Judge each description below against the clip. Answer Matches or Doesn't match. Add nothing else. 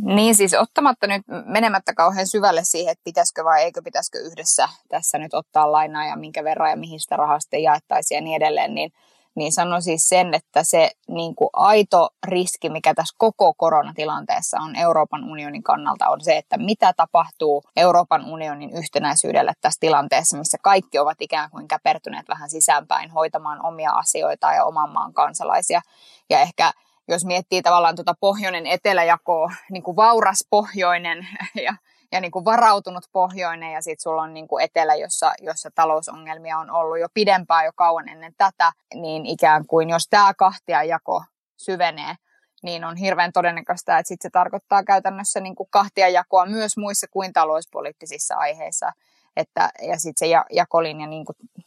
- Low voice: Doesn't match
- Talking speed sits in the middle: Doesn't match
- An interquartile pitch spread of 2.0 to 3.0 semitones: Doesn't match